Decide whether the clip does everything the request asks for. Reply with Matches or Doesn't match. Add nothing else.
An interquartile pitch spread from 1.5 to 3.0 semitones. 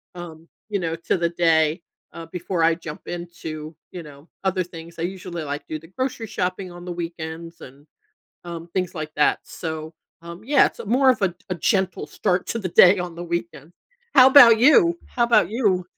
Matches